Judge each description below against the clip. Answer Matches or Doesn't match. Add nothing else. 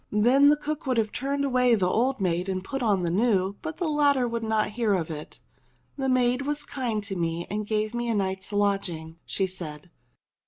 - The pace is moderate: Doesn't match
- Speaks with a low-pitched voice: Doesn't match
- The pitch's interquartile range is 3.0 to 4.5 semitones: Doesn't match